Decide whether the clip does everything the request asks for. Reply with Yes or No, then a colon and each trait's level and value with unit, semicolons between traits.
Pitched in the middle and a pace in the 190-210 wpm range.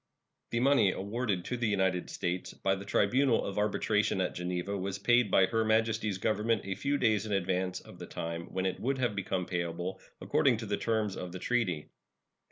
No: low, 100 Hz; average, 195 wpm